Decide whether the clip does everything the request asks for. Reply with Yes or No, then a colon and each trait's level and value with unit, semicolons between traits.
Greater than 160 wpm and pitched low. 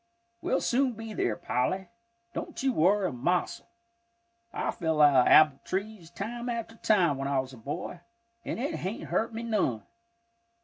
No: average, 170 wpm; medium, 185 Hz